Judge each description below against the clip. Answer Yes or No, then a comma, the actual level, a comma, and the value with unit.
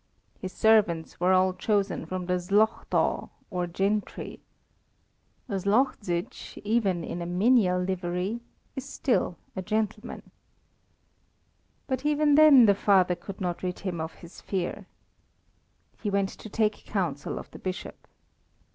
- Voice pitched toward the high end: Yes, high, 195 Hz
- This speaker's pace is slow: Yes, slow, 130 wpm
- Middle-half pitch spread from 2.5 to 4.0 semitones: Yes, average, 3.3 semitones